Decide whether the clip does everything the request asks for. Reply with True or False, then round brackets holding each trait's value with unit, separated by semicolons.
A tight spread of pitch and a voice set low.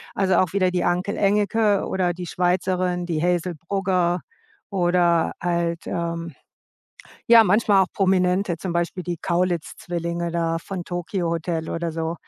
False (1.6 semitones; 175 Hz)